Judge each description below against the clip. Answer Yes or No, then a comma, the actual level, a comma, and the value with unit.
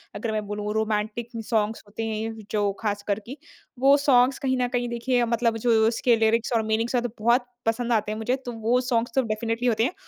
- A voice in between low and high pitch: No, high, 230 Hz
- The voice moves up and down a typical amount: No, narrow, 2.0 semitones